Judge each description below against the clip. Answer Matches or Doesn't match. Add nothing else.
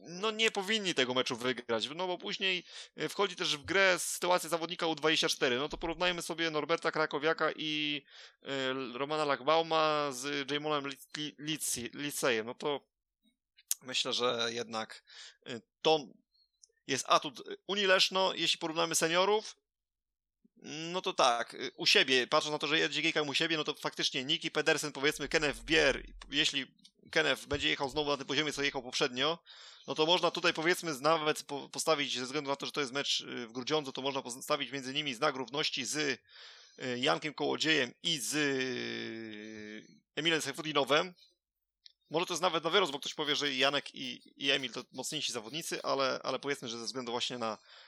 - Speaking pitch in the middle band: Matches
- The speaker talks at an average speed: Doesn't match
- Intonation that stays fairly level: Doesn't match